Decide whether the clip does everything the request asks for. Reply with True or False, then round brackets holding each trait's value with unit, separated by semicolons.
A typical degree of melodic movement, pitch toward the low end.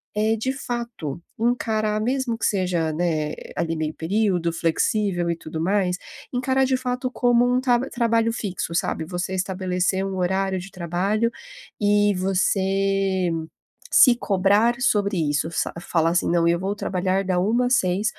False (4.3 semitones; 195 Hz)